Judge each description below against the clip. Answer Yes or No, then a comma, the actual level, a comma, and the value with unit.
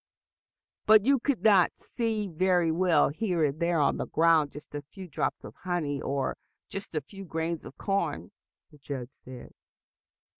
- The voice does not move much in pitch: No, average, 4.8 semitones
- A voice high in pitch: No, medium, 170 Hz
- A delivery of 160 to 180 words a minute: Yes, average, 165 wpm